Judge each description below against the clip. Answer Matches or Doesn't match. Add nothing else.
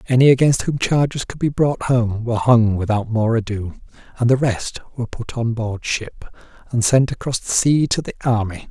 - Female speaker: Doesn't match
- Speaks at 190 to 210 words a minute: Matches